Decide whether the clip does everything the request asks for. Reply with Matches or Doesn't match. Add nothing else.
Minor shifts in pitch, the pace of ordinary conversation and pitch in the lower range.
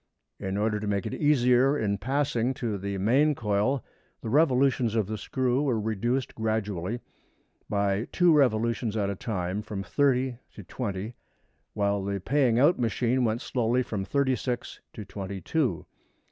Doesn't match